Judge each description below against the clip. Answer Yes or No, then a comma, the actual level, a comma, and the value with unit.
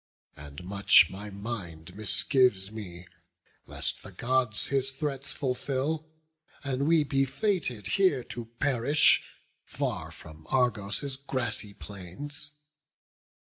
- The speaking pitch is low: Yes, low, 125 Hz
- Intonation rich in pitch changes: Yes, wide, 5.7 semitones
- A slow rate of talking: Yes, slow, 105 wpm